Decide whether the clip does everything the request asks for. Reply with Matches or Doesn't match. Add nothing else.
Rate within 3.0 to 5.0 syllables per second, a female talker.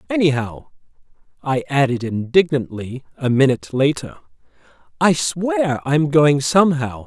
Doesn't match